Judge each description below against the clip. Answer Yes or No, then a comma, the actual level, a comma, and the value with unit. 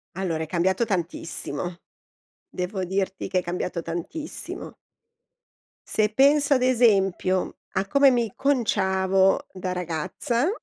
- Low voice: No, high, 190 Hz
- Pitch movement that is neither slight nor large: Yes, average, 4.7 semitones